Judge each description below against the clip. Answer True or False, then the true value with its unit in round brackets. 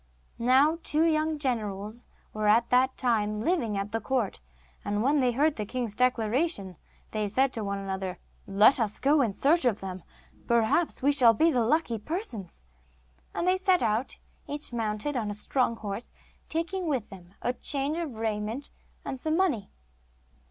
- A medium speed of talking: True (175 wpm)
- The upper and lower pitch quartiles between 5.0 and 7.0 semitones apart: True (5.6 semitones)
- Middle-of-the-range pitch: False (240 Hz)